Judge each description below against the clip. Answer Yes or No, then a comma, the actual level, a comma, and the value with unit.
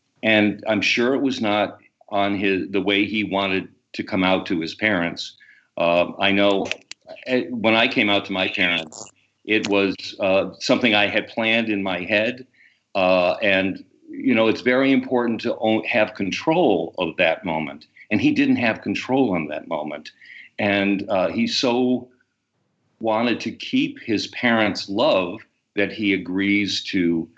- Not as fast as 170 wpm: Yes, average, 160 wpm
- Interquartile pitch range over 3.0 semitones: Yes, average, 4.2 semitones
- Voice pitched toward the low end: Yes, low, 105 Hz